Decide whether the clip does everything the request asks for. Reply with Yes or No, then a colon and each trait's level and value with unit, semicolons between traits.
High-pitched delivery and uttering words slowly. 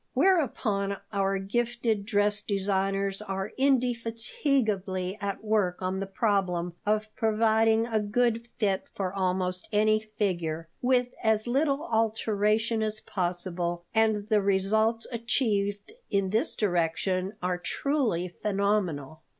Yes: high, 210 Hz; slow, 115 wpm